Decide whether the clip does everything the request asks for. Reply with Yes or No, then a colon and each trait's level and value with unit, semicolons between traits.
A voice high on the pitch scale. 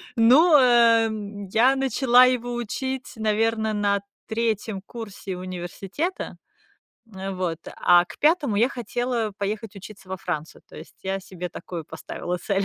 Yes: high, 220 Hz